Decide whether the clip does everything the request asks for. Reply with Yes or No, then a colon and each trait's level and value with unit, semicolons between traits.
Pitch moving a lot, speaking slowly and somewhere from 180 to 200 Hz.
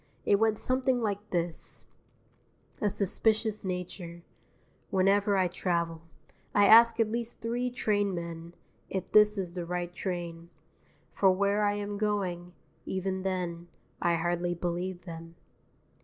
No: average, 3.2 semitones; slow, 130 wpm; high, 190 Hz